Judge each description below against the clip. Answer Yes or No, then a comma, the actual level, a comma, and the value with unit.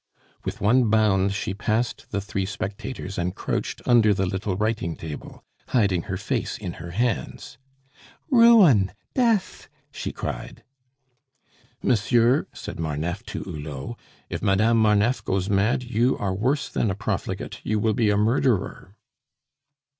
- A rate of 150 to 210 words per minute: No, average, 140 wpm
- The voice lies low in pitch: Yes, low, 105 Hz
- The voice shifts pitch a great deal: No, average, 3.7 semitones